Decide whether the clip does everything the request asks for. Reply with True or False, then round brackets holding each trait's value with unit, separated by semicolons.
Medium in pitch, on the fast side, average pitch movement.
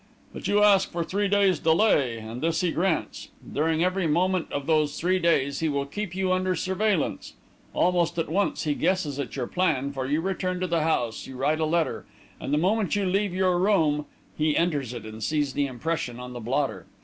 True (165 Hz; 210 wpm; 4.6 semitones)